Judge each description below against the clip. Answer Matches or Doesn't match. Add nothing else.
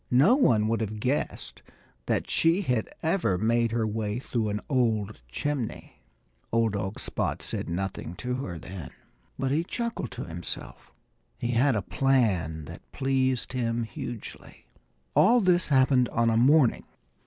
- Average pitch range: Matches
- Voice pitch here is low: Matches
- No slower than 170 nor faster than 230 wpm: Doesn't match